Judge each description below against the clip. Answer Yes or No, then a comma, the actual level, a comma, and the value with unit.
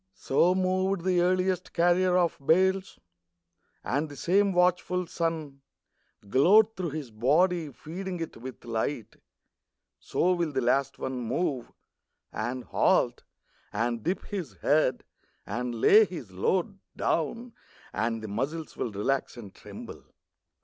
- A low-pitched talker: No, medium, 160 Hz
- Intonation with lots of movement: Yes, wide, 6.5 semitones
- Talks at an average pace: No, slow, 130 wpm